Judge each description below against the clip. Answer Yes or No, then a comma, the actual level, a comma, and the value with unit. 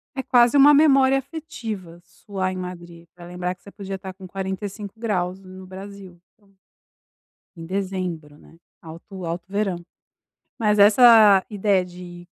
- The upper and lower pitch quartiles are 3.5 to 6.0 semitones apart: No, average, 2.8 semitones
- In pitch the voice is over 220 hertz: No, high, 190 Hz